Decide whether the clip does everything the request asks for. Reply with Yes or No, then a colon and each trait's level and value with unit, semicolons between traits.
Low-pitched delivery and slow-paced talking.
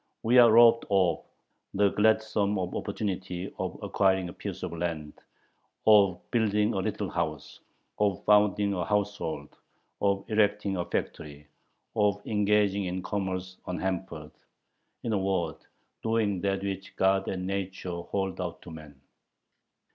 Yes: very low, 95 Hz; slow, 130 wpm